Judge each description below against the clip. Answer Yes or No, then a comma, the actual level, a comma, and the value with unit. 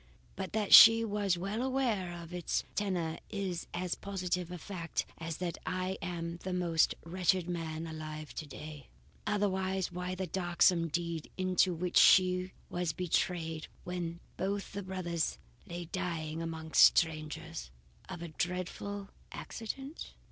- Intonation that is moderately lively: No, narrow, 2.3 semitones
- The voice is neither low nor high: Yes, medium, 180 Hz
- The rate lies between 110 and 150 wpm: Yes, slow, 135 wpm